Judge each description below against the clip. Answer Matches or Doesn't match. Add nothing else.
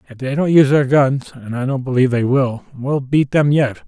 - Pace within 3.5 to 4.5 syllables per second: Doesn't match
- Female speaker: Doesn't match